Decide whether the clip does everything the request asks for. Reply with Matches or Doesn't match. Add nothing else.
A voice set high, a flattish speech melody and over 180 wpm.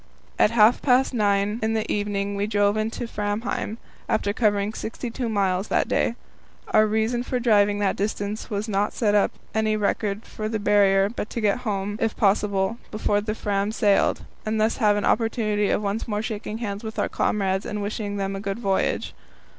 Matches